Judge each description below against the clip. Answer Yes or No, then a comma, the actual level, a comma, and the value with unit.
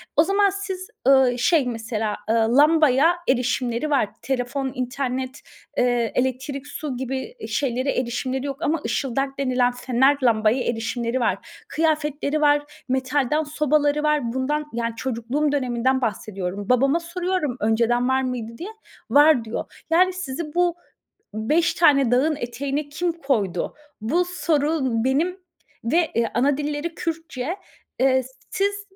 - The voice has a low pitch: No, very high, 270 Hz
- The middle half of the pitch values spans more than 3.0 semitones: Yes, average, 3.8 semitones